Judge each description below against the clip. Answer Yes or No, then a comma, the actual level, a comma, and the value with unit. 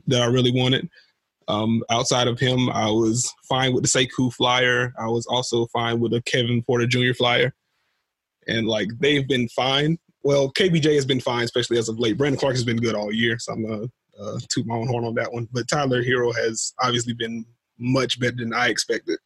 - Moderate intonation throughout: No, narrow, 1.9 semitones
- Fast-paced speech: Yes, fast, 215 wpm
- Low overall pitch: Yes, low, 125 Hz